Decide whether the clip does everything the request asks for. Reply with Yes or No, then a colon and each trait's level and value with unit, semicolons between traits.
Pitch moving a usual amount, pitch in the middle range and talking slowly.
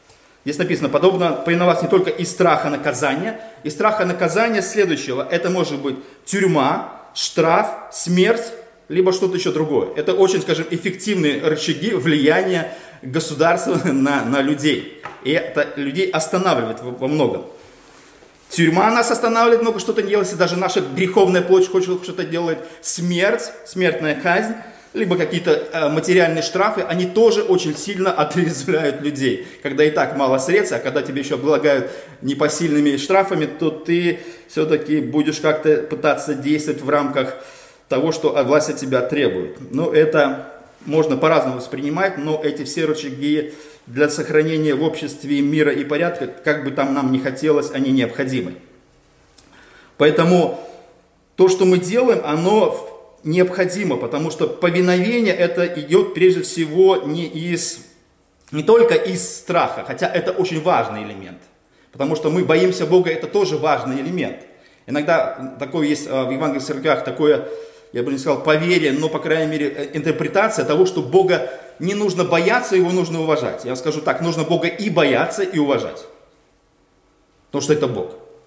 No: average, 3.9 semitones; medium, 165 Hz; average, 145 wpm